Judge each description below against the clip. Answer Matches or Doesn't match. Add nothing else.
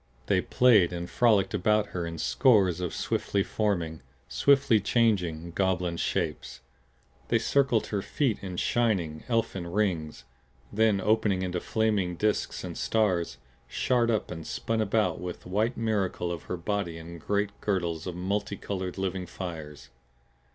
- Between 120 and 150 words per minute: Matches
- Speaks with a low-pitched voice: Matches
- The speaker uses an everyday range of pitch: Matches